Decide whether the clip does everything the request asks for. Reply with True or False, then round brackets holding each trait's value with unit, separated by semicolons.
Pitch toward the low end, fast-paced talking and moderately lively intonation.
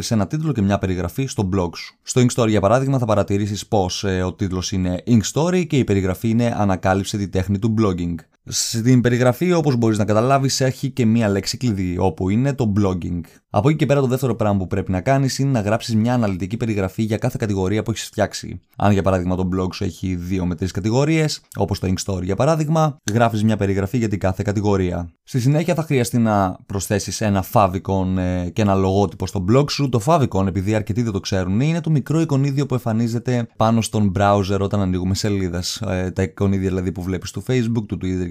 True (105 Hz; 210 wpm; 4.6 semitones)